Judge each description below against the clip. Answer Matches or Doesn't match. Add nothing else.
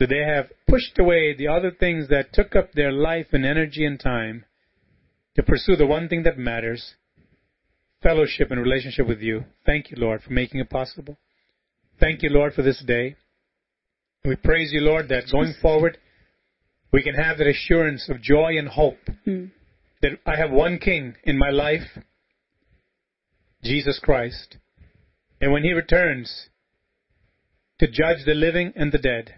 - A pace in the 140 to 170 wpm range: Matches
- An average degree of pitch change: Matches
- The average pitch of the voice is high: Doesn't match